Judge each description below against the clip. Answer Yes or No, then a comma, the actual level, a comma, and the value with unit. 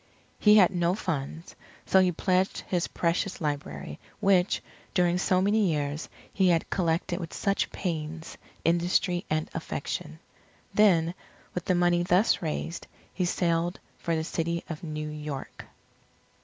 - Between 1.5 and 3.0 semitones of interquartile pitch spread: Yes, narrow, 2.4 semitones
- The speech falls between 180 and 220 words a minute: No, average, 140 wpm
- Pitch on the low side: No, medium, 175 Hz